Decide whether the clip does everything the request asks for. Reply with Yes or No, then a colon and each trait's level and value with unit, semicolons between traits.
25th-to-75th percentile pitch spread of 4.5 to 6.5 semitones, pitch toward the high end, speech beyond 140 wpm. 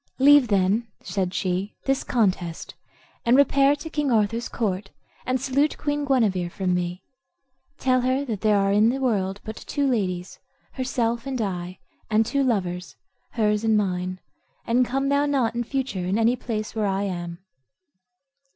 Yes: average, 5.3 semitones; high, 220 Hz; average, 160 wpm